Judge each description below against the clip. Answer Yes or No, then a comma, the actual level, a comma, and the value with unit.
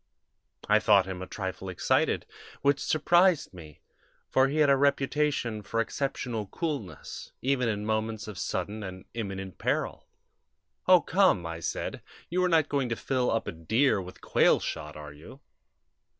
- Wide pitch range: Yes, wide, 6.9 semitones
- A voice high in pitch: No, low, 110 Hz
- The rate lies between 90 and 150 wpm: No, average, 160 wpm